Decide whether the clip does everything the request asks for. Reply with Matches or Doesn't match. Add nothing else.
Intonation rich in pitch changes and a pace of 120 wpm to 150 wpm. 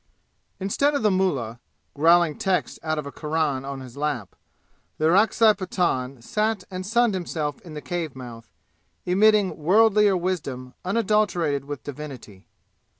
Matches